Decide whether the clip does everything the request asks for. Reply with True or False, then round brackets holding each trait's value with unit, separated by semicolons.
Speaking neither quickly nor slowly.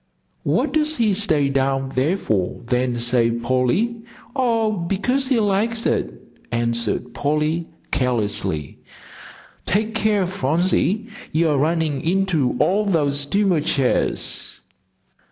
False (110 wpm)